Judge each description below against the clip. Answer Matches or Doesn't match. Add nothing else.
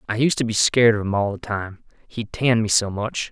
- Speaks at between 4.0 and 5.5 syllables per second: Doesn't match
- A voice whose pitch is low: Matches